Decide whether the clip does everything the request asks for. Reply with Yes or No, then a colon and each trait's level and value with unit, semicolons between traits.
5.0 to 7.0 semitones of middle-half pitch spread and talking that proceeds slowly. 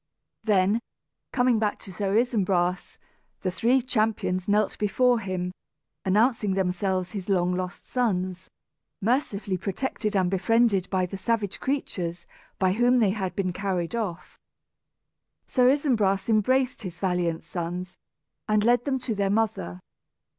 No: average, 3.9 semitones; slow, 130 wpm